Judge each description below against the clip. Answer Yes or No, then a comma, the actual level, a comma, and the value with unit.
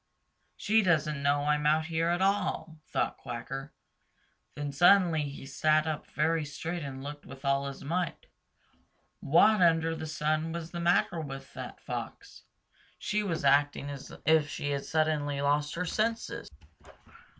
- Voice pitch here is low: No, medium, 155 Hz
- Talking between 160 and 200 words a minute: No, average, 150 wpm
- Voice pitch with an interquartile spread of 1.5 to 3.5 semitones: Yes, average, 2.9 semitones